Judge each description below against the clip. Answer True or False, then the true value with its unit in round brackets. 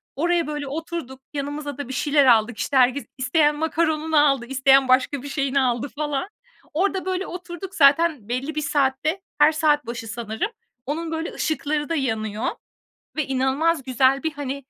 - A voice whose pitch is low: False (285 Hz)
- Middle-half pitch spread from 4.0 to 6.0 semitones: False (3.2 semitones)